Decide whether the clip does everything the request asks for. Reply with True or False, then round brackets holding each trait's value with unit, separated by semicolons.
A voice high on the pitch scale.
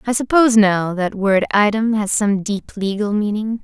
True (210 Hz)